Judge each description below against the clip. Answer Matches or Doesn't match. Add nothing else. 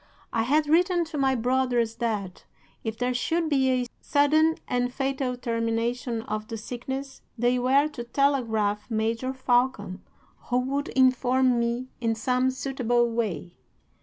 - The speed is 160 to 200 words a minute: Doesn't match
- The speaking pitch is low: Doesn't match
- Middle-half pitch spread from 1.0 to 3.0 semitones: Matches